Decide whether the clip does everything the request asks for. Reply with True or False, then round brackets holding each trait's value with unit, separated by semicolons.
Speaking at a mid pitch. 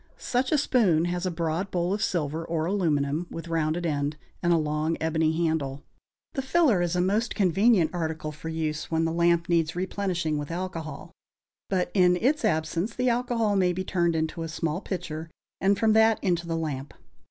True (170 Hz)